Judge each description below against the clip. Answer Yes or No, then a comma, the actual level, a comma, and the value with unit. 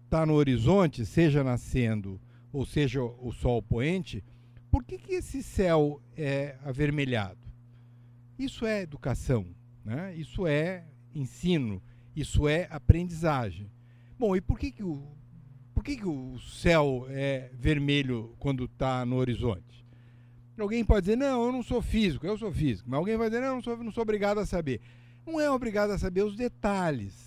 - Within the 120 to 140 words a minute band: No, average, 165 wpm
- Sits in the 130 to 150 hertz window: Yes, medium, 140 Hz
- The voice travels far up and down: Yes, wide, 7.7 semitones